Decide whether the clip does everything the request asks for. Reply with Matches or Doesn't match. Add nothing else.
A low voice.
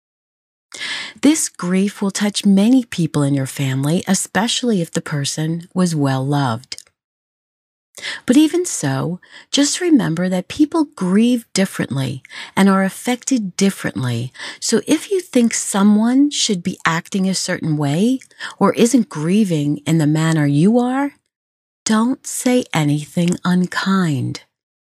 Doesn't match